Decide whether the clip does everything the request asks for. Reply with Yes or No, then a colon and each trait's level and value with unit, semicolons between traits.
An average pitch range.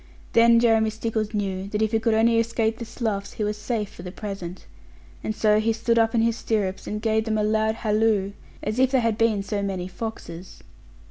No: narrow, 1.7 semitones